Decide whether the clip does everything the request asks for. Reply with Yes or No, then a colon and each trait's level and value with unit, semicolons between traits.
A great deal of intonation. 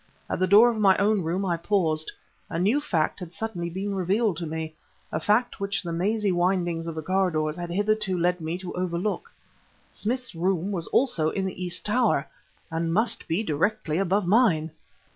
No: average, 3.6 semitones